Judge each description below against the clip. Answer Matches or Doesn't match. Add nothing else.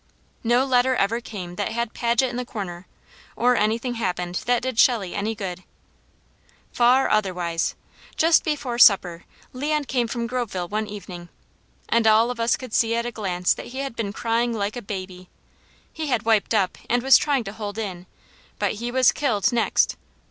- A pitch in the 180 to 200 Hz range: Doesn't match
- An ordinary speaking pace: Matches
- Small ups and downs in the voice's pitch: Doesn't match